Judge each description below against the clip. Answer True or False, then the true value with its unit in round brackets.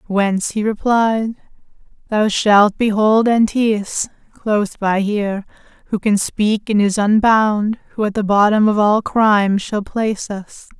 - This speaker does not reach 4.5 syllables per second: True (4.1 syllables/s)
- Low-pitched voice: False (210 Hz)